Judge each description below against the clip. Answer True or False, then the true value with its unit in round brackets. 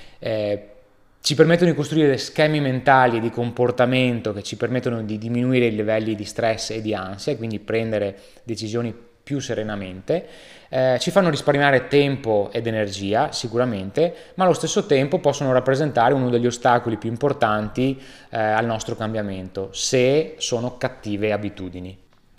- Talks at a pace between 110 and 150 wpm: True (145 wpm)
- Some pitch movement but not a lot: True (3.8 semitones)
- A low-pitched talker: True (120 Hz)